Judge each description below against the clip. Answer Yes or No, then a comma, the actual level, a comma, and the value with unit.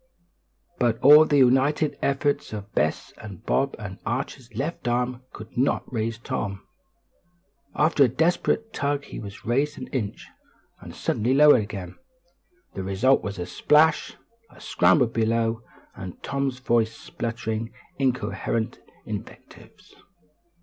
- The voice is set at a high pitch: No, low, 125 Hz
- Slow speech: Yes, slow, 130 wpm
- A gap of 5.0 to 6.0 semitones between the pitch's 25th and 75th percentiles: No, average, 4.2 semitones